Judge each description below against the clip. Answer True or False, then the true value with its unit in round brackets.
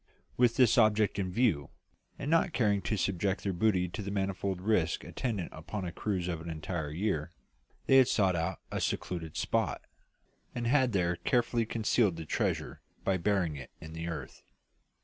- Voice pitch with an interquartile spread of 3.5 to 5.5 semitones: True (4.3 semitones)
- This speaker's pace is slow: False (175 wpm)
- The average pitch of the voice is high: False (95 Hz)